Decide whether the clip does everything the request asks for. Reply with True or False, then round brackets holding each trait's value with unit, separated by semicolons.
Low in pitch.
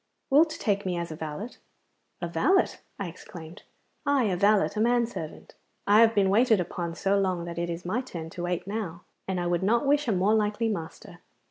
False (195 Hz)